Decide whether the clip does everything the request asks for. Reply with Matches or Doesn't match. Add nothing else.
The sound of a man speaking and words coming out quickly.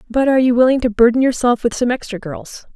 Doesn't match